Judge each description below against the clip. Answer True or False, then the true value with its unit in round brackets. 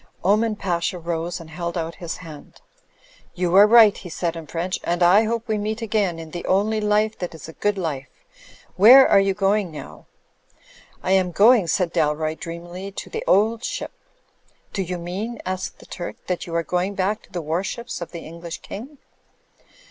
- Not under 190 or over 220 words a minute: True (195 wpm)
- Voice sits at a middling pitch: True (180 Hz)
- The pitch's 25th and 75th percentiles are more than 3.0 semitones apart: True (3.7 semitones)